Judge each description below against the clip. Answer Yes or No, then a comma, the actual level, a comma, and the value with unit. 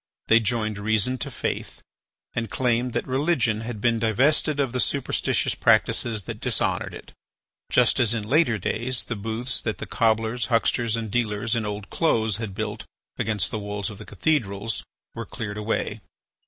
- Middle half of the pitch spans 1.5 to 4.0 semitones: Yes, narrow, 2.4 semitones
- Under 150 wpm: No, average, 165 wpm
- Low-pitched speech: Yes, low, 115 Hz